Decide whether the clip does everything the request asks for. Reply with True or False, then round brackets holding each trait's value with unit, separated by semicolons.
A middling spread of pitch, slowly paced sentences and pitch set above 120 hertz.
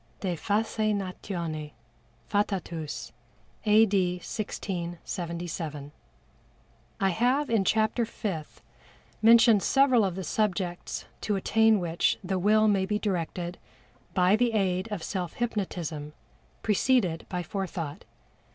True (3.8 semitones; 105 wpm; 190 Hz)